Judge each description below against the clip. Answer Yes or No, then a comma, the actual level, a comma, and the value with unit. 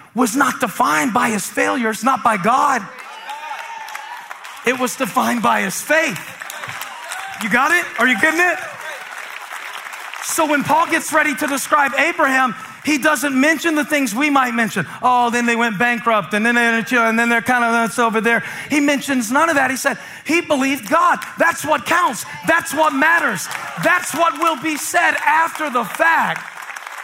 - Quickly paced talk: No, average, 175 wpm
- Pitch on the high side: Yes, very high, 280 Hz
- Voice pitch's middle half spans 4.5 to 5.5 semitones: Yes, average, 5.1 semitones